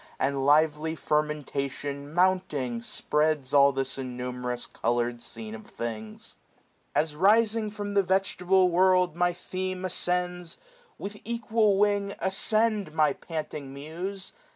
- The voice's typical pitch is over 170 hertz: No, medium, 160 Hz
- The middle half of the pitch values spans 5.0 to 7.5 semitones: Yes, wide, 5.4 semitones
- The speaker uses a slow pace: Yes, slow, 120 wpm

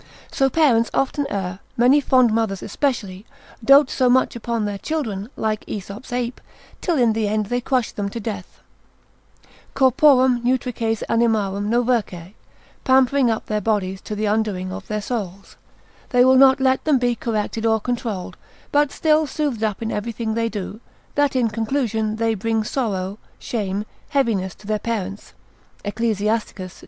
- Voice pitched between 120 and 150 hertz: No, high, 225 Hz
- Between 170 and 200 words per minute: No, average, 155 wpm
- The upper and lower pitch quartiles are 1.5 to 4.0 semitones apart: Yes, average, 3.5 semitones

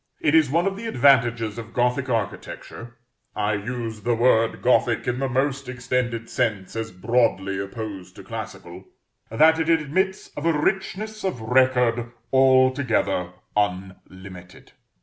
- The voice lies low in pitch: Yes, low, 120 Hz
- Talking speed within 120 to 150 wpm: Yes, slow, 135 wpm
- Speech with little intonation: No, average, 3.7 semitones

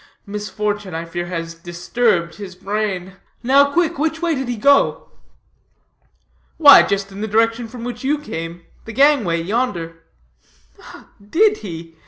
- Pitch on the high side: Yes, high, 210 Hz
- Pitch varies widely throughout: Yes, wide, 7.2 semitones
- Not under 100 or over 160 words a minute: Yes, average, 140 wpm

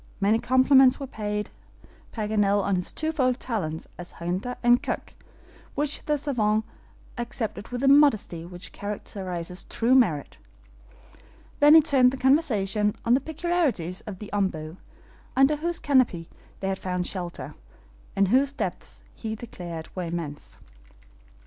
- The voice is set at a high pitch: Yes, high, 215 Hz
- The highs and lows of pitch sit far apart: Yes, wide, 6.5 semitones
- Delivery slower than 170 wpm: Yes, slow, 135 wpm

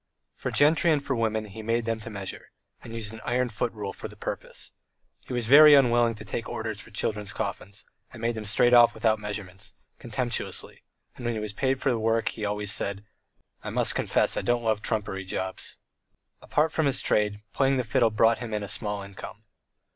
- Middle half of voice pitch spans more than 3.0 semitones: No, narrow, 2.6 semitones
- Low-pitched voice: Yes, low, 110 Hz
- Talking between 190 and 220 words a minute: Yes, fast, 205 wpm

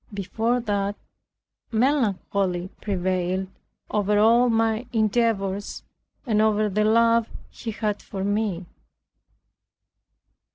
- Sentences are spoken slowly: Yes, slow, 90 wpm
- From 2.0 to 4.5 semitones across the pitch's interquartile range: Yes, narrow, 2.5 semitones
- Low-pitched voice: No, high, 210 Hz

